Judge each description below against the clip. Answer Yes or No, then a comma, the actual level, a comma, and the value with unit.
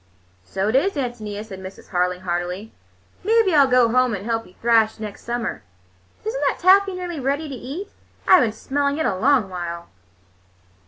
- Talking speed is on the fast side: No, average, 180 wpm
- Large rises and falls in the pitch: Yes, wide, 6.5 semitones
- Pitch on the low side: No, high, 235 Hz